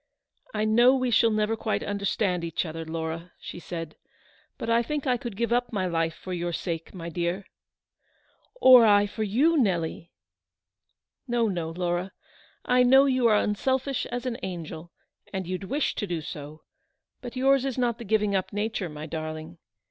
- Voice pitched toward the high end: Yes, high, 200 Hz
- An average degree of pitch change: No, wide, 6.0 semitones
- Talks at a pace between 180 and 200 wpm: Yes, average, 185 wpm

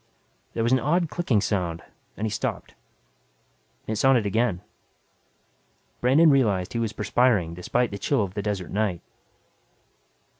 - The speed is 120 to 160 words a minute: Yes, average, 140 wpm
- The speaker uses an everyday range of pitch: Yes, average, 4.4 semitones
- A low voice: Yes, low, 110 Hz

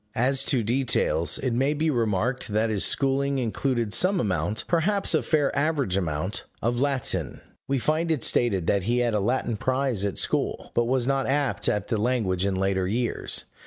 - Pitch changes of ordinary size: Yes, average, 5.0 semitones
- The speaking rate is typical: Yes, average, 185 wpm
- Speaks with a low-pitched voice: Yes, low, 120 Hz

